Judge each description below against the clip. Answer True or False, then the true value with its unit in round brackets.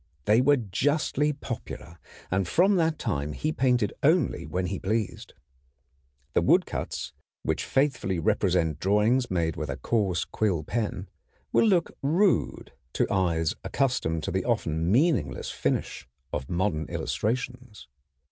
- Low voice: True (105 Hz)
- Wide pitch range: True (7.7 semitones)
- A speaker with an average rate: False (130 wpm)